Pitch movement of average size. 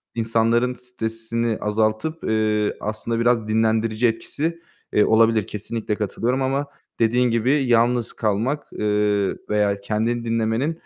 No: narrow, 1.9 semitones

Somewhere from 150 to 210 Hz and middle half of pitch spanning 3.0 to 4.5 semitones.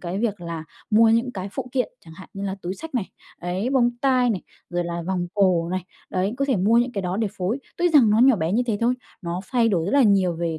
No: high, 200 Hz; average, 5.1 semitones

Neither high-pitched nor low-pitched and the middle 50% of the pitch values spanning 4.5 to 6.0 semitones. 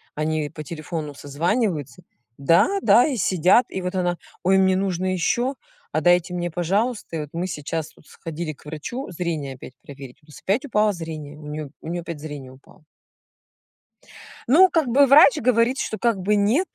Yes: medium, 175 Hz; wide, 5.5 semitones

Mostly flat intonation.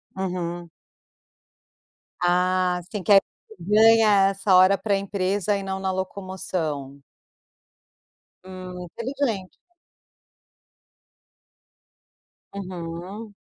Yes: narrow, 1.8 semitones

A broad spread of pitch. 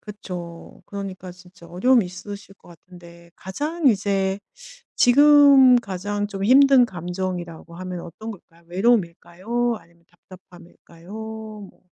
No: average, 4.0 semitones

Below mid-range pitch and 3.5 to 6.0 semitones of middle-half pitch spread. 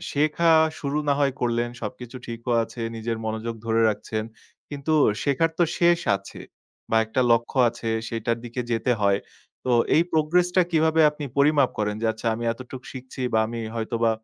Yes: low, 120 Hz; average, 4.4 semitones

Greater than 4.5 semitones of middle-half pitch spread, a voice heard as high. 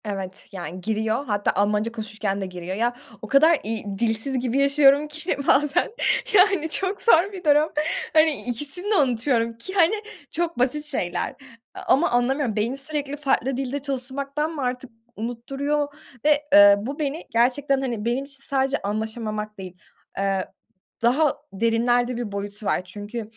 Yes: average, 5.2 semitones; very high, 250 Hz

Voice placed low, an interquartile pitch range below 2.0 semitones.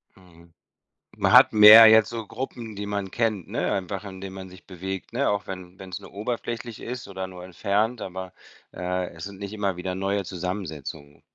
No: very low, 95 Hz; narrow, 2.5 semitones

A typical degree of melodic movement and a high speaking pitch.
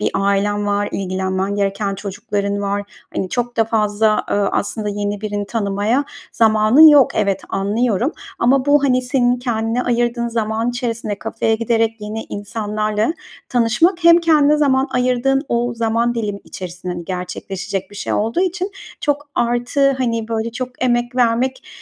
Yes: average, 3.4 semitones; high, 225 Hz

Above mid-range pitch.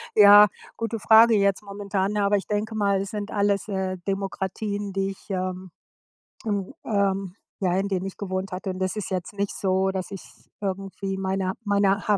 Yes: high, 195 Hz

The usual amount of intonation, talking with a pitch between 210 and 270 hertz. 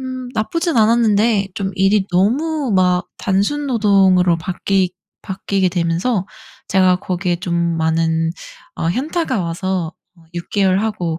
No: average, 3.9 semitones; high, 190 Hz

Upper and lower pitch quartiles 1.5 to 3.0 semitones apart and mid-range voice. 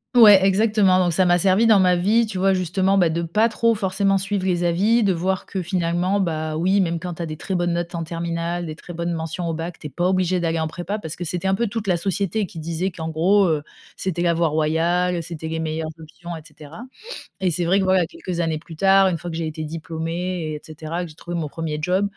Yes: average, 2.7 semitones; medium, 175 Hz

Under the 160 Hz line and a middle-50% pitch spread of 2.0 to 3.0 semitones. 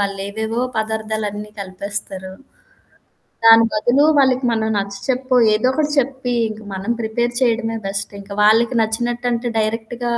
No: high, 220 Hz; narrow, 2.6 semitones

